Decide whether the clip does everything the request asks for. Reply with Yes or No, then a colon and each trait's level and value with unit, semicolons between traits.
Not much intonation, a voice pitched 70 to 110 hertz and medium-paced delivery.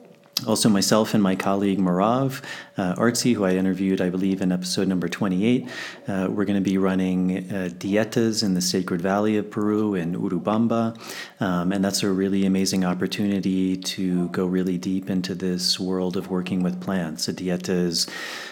Yes: narrow, 1.6 semitones; very low, 95 Hz; average, 170 wpm